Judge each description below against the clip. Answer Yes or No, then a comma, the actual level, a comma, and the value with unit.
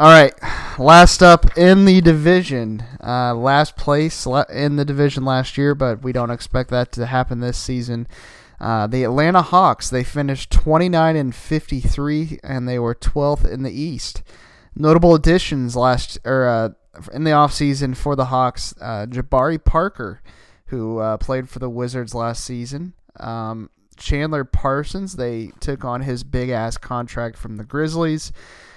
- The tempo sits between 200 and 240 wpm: No, average, 155 wpm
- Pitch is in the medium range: No, low, 130 Hz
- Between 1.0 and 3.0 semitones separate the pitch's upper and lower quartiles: No, average, 3.8 semitones